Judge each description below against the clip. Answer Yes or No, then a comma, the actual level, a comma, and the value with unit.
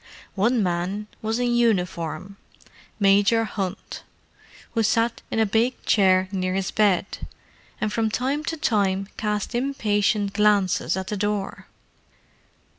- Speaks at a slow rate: Yes, slow, 125 wpm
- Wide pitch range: No, average, 2.8 semitones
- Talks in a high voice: Yes, high, 210 Hz